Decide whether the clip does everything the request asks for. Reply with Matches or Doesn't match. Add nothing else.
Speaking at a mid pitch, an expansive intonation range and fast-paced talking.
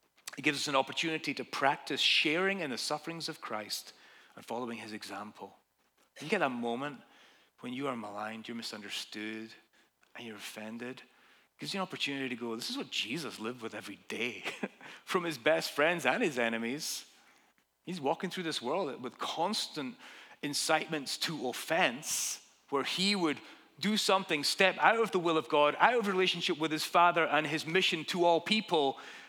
Doesn't match